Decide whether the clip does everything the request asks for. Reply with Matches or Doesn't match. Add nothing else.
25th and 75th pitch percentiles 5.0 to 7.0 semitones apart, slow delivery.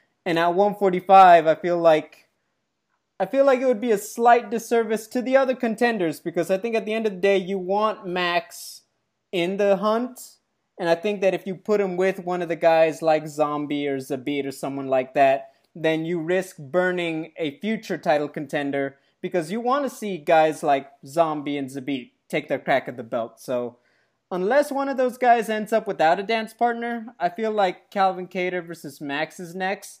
Doesn't match